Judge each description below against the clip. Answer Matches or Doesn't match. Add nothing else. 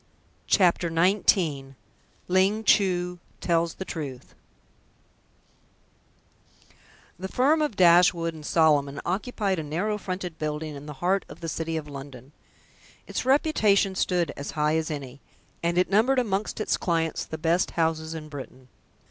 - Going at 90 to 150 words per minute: Matches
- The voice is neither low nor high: Matches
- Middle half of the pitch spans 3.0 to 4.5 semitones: Matches